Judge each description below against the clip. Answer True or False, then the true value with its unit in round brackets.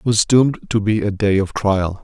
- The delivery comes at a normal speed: False (265 wpm)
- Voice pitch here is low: True (105 Hz)